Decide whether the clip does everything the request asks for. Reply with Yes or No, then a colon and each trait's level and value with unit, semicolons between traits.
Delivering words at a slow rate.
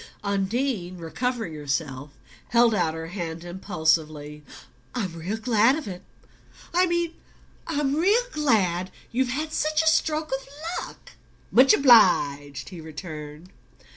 Yes: slow, 125 wpm